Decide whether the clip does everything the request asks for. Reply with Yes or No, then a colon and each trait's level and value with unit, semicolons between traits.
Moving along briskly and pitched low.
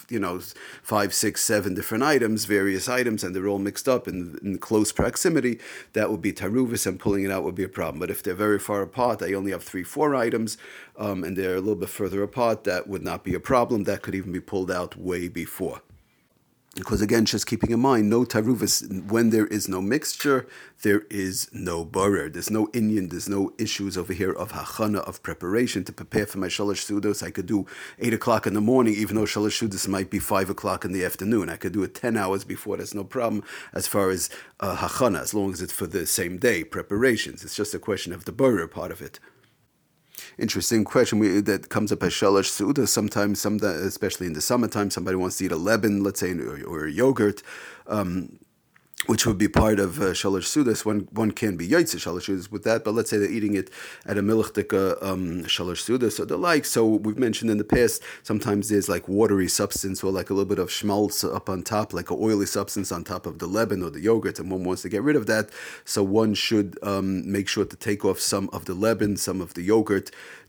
Yes: fast, 225 wpm; low, 100 Hz